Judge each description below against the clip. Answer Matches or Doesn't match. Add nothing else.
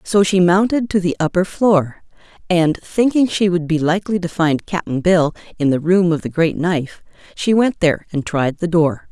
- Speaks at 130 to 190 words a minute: Doesn't match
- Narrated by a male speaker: Doesn't match